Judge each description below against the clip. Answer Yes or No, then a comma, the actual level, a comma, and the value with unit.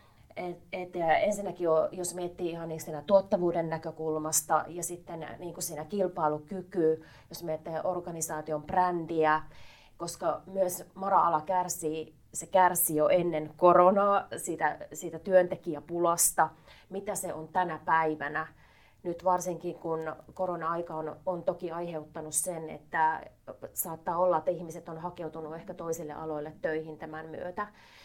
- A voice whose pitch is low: No, medium, 165 Hz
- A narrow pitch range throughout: Yes, narrow, 2.3 semitones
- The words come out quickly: No, average, 130 wpm